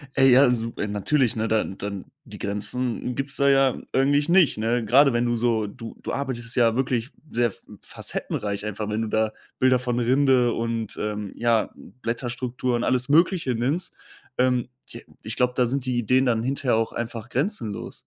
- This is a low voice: Yes, low, 120 Hz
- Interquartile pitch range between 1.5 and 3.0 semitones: Yes, narrow, 2.6 semitones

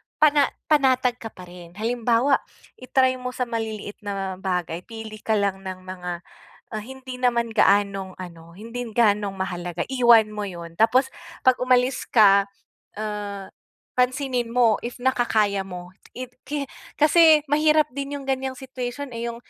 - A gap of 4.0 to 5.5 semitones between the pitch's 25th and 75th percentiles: Yes, average, 4.6 semitones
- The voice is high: Yes, high, 230 Hz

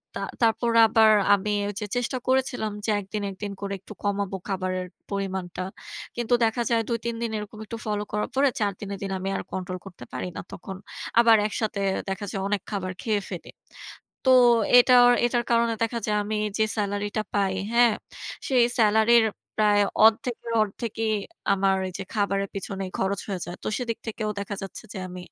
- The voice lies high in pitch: Yes, high, 210 Hz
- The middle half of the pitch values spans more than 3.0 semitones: No, average, 2.7 semitones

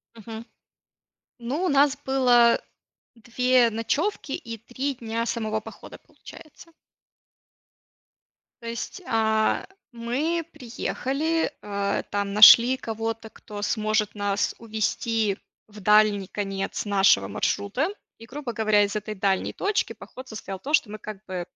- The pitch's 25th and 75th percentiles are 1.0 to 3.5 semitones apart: Yes, average, 3.2 semitones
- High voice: Yes, high, 225 Hz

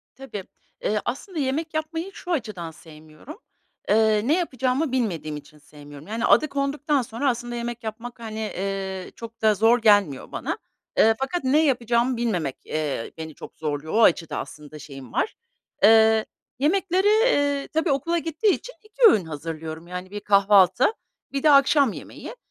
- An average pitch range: No, wide, 7.6 semitones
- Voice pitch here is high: Yes, high, 225 Hz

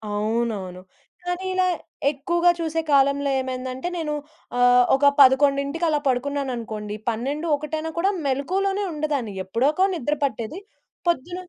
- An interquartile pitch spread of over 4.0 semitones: Yes, average, 4.7 semitones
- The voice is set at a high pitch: Yes, very high, 280 Hz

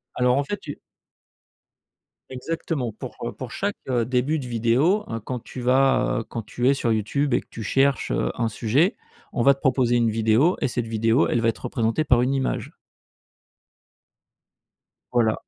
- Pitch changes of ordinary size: Yes, average, 3.1 semitones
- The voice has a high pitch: No, low, 125 Hz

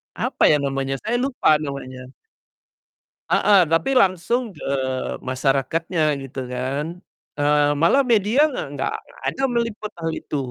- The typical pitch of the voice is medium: Yes, medium, 160 Hz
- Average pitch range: No, wide, 7.6 semitones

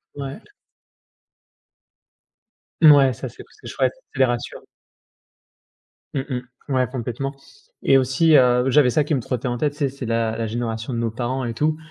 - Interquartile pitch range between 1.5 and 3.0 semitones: Yes, narrow, 2.6 semitones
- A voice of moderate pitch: No, low, 130 Hz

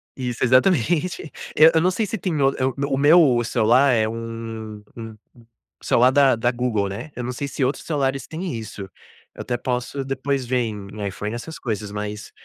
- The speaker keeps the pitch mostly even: No, average, 3.9 semitones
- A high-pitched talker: No, low, 125 Hz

